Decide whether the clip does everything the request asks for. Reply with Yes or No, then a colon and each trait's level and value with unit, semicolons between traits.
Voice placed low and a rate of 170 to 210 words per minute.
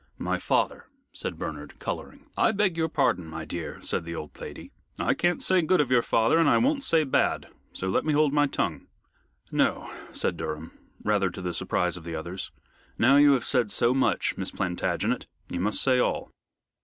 Yes: low, 120 Hz; average, 195 wpm